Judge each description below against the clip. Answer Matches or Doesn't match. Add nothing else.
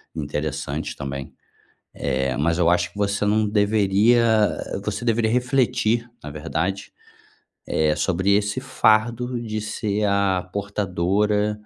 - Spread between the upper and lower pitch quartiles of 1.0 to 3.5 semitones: Doesn't match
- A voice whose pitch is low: Matches